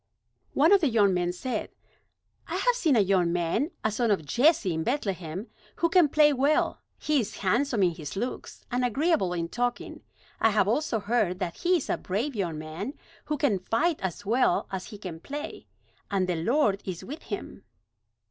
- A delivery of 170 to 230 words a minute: Yes, average, 190 wpm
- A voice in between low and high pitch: No, high, 220 Hz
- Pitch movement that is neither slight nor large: No, wide, 7.7 semitones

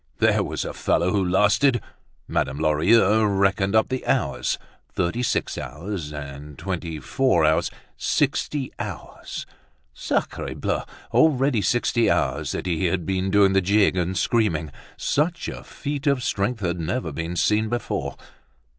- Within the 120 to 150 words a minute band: Yes, average, 145 wpm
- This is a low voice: Yes, very low, 95 Hz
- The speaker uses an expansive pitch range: Yes, wide, 5.8 semitones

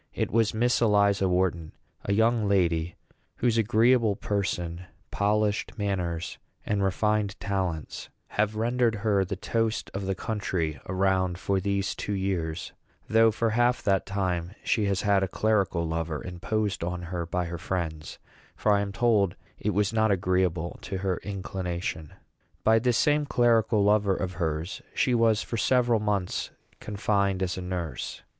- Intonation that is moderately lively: Yes, average, 3.3 semitones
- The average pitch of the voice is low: Yes, low, 100 Hz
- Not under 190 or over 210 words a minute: No, average, 155 wpm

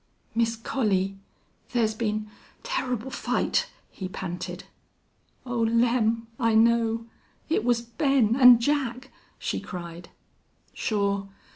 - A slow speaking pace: Yes, slow, 105 wpm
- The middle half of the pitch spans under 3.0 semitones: Yes, narrow, 2.5 semitones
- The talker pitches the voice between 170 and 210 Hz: No, high, 230 Hz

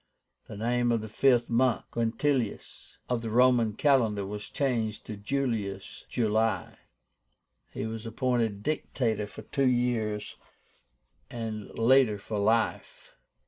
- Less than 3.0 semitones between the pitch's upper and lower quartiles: Yes, narrow, 2.5 semitones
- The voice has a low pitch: Yes, low, 115 Hz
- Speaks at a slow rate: Yes, slow, 120 wpm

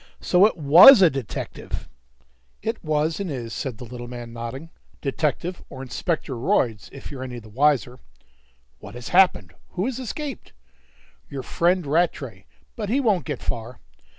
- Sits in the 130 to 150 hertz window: Yes, medium, 140 Hz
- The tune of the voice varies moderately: No, wide, 6.4 semitones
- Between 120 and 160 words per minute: Yes, average, 155 wpm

